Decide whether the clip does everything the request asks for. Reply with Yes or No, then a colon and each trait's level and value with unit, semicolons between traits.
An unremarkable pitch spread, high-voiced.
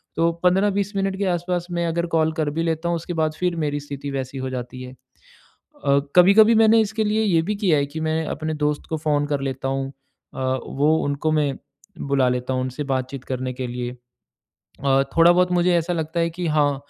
No: average, 4.4 semitones; medium, 155 Hz